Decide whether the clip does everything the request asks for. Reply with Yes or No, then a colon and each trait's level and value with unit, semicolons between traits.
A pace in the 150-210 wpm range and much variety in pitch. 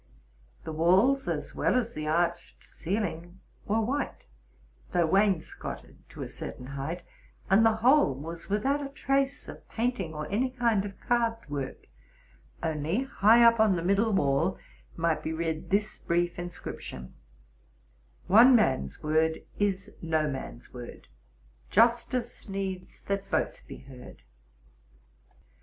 No: average, 140 wpm; wide, 6.1 semitones